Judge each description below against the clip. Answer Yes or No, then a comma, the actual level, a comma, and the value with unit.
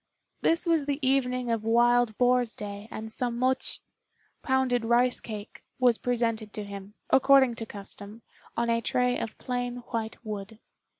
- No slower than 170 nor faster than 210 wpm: No, average, 155 wpm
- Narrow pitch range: Yes, narrow, 2.3 semitones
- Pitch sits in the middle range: No, high, 235 Hz